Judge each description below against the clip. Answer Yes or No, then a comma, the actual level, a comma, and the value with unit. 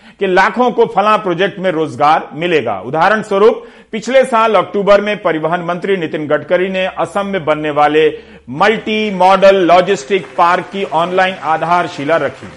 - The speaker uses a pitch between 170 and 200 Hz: Yes, medium, 185 Hz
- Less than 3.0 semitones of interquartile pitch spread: No, average, 3.6 semitones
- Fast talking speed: No, average, 150 wpm